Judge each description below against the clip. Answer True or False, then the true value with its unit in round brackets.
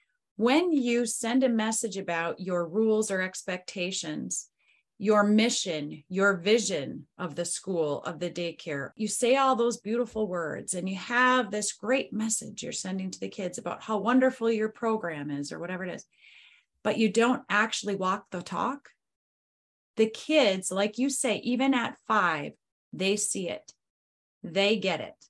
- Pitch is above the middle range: True (210 Hz)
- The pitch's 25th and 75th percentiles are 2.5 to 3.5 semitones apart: False (4.2 semitones)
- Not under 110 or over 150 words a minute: False (160 wpm)